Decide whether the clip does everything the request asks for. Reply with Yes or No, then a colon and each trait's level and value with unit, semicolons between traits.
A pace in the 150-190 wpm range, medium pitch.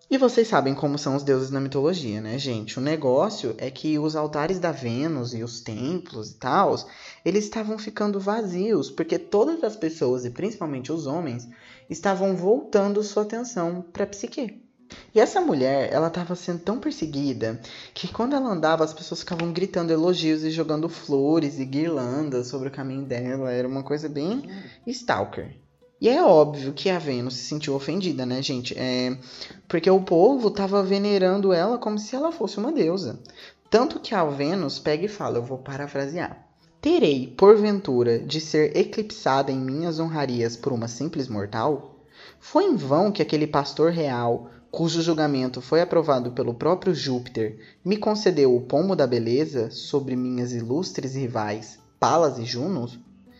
Yes: average, 165 wpm; medium, 155 Hz